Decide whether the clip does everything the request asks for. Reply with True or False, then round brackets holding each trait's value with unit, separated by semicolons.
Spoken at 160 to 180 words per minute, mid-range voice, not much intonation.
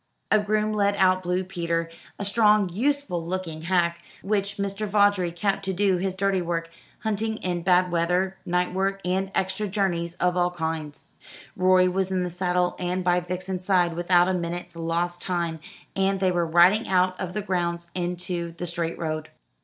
True (175 wpm; 180 Hz; 2.0 semitones)